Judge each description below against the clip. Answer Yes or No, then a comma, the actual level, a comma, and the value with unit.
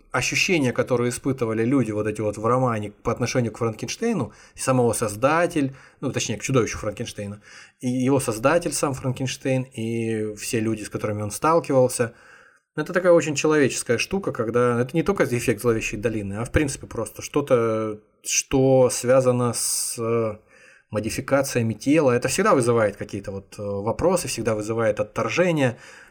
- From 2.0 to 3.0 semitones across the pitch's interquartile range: No, average, 3.4 semitones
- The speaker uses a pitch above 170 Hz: No, low, 120 Hz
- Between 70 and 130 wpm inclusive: No, average, 145 wpm